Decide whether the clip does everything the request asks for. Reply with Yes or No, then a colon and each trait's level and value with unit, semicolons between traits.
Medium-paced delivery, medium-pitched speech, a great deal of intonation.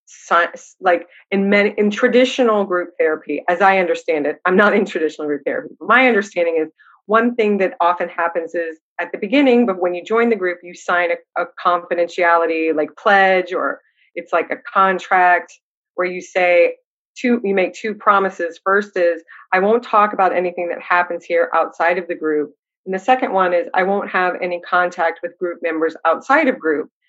No: average, 190 wpm; medium, 180 Hz; average, 3.1 semitones